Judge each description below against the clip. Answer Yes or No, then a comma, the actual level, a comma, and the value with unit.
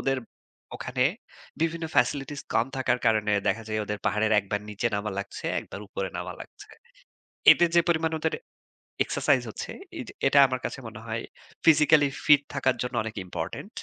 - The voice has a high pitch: No, low, 125 Hz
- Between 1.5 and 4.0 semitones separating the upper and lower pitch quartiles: No, wide, 5.4 semitones